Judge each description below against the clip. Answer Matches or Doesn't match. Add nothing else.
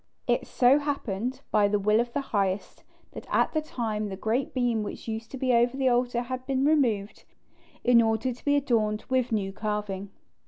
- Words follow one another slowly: Doesn't match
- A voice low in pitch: Doesn't match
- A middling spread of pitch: Matches